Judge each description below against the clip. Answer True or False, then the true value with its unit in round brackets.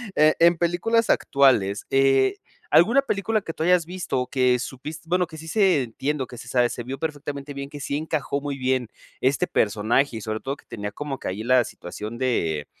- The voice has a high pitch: False (140 Hz)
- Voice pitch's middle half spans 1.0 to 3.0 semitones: False (4.5 semitones)